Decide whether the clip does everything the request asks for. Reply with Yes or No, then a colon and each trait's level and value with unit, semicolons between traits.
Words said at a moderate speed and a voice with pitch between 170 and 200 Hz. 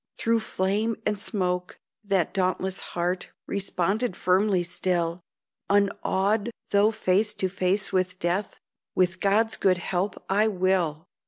No: slow, 120 wpm; high, 190 Hz